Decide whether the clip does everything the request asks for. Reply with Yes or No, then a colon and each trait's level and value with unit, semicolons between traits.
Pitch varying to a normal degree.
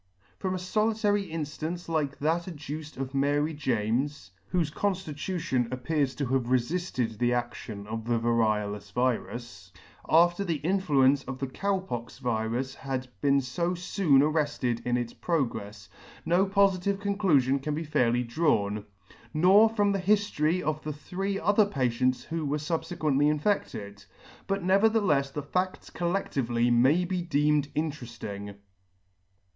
No: wide, 6.3 semitones